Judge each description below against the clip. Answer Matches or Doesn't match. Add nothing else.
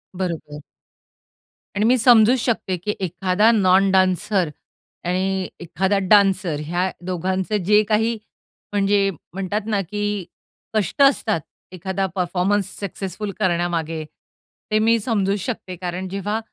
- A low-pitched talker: Doesn't match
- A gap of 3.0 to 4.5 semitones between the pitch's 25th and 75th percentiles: Doesn't match